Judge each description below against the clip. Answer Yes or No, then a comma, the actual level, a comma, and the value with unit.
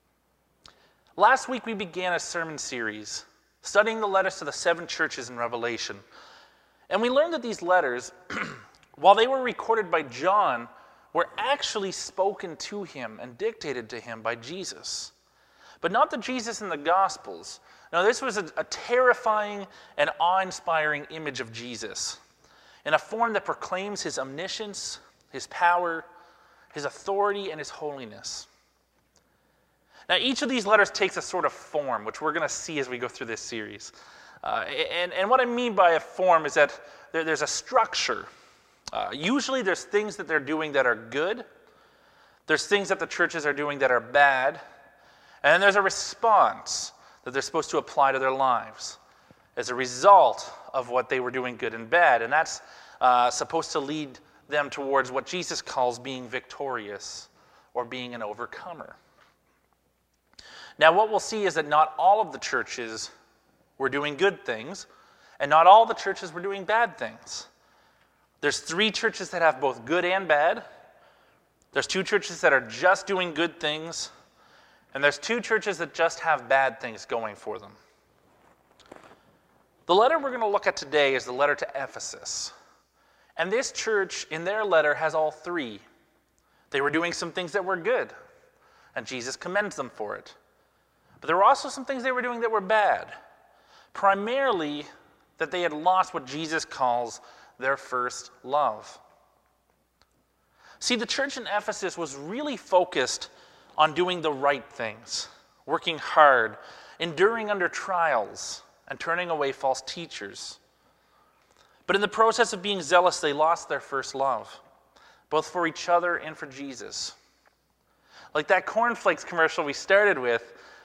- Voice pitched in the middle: Yes, medium, 175 Hz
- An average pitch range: No, wide, 6.4 semitones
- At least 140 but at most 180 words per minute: Yes, average, 165 wpm